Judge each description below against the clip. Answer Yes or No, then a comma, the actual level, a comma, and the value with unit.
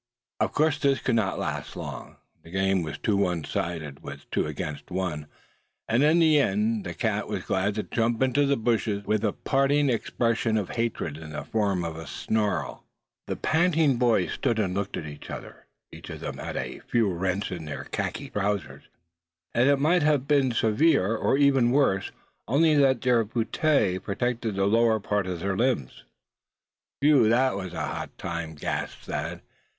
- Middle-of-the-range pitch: No, low, 110 Hz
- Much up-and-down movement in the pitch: Yes, wide, 5.9 semitones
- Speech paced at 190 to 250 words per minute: No, average, 175 wpm